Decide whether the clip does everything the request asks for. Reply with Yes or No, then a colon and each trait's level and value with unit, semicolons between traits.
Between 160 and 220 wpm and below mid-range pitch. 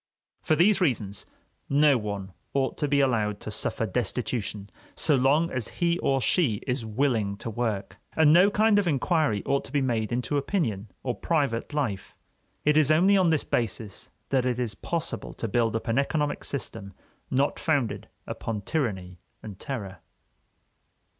Yes: average, 165 wpm; low, 125 Hz